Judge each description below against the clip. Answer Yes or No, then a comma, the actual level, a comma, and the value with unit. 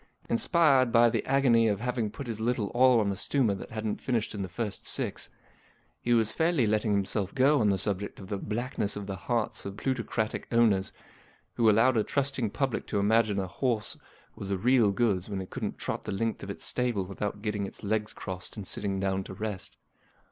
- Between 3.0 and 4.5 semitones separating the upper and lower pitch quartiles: Yes, average, 3.3 semitones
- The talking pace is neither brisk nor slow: No, fast, 210 wpm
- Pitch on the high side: No, low, 110 Hz